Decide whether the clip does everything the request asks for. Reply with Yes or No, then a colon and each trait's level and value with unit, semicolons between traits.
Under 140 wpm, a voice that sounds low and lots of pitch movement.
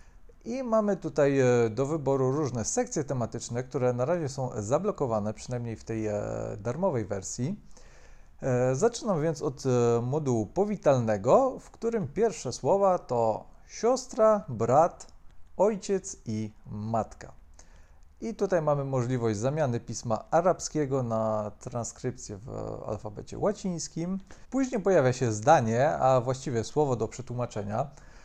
Yes: average, 115 wpm; low, 130 Hz; wide, 6.8 semitones